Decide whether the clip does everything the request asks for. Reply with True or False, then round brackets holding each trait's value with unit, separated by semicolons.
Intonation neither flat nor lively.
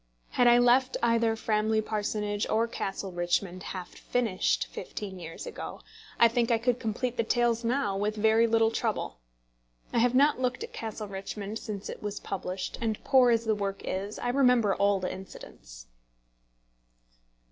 True (3.2 semitones)